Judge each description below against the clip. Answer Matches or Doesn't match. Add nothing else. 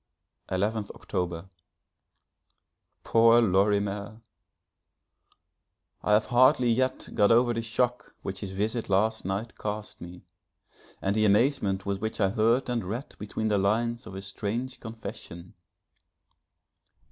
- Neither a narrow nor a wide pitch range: Matches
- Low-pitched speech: Matches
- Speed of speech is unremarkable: Doesn't match